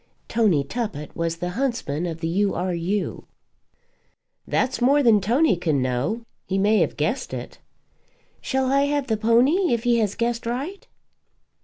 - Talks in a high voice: Yes, high, 220 Hz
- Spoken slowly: No, average, 160 wpm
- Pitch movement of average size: No, wide, 6.4 semitones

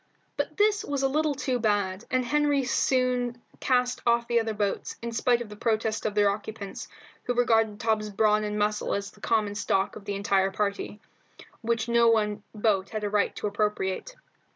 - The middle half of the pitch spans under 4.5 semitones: Yes, average, 2.9 semitones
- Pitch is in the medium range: No, high, 220 Hz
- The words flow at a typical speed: Yes, average, 190 wpm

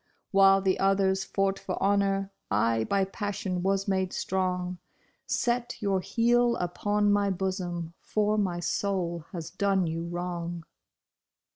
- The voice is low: No, high, 190 Hz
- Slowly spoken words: Yes, slow, 130 wpm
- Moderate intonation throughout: No, narrow, 2.2 semitones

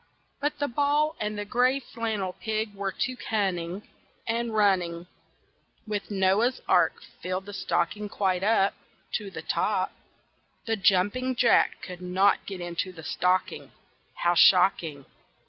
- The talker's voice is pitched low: No, high, 200 Hz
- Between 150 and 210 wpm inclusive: No, slow, 135 wpm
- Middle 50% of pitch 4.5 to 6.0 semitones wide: No, average, 3.8 semitones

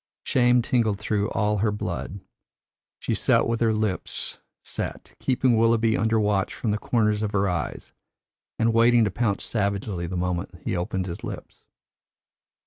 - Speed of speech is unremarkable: Yes, average, 155 wpm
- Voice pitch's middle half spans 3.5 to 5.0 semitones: No, average, 2.8 semitones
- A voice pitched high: No, low, 105 Hz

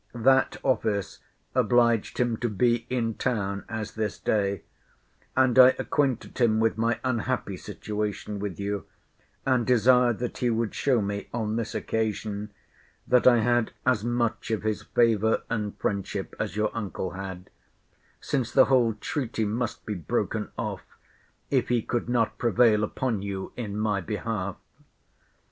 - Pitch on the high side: No, low, 110 Hz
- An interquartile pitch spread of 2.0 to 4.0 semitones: Yes, average, 2.7 semitones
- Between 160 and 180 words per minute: No, average, 150 wpm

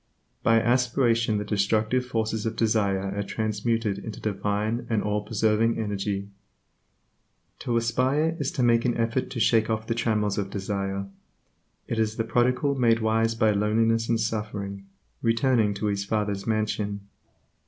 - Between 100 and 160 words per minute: Yes, average, 150 wpm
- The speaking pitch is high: No, low, 110 Hz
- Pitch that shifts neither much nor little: No, narrow, 2.0 semitones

